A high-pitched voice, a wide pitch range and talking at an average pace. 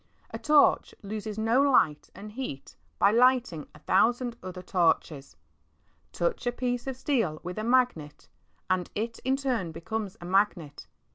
Yes: high, 215 Hz; wide, 6.0 semitones; average, 150 wpm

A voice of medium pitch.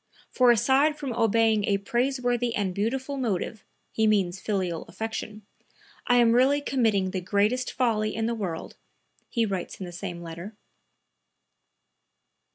No: high, 220 Hz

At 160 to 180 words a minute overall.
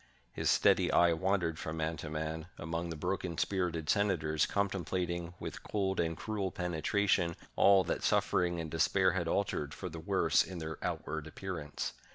Yes: average, 170 wpm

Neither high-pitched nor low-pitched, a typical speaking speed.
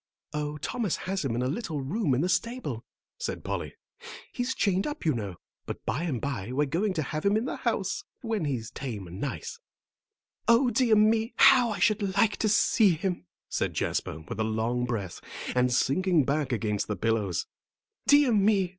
Yes: medium, 155 Hz; average, 190 wpm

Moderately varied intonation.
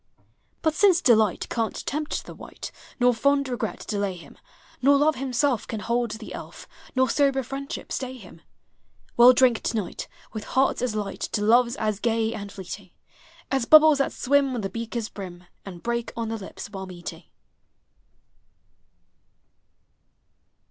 Yes: average, 4.2 semitones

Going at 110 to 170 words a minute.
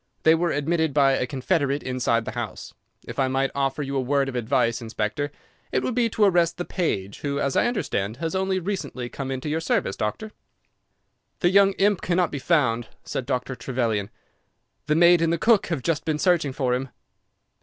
No: average, 195 wpm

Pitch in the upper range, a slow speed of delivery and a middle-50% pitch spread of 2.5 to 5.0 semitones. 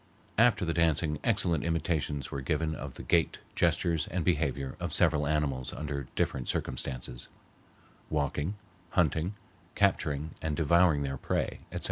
No: very low, 75 Hz; slow, 130 wpm; average, 2.9 semitones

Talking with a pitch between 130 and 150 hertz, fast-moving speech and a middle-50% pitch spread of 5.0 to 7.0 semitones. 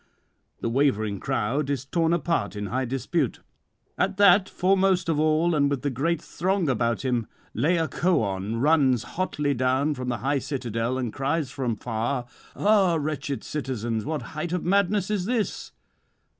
No: medium, 140 Hz; average, 155 wpm; wide, 5.5 semitones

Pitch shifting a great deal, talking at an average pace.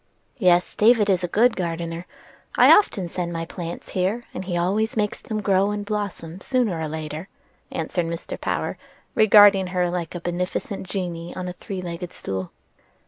No: average, 3.1 semitones; average, 180 wpm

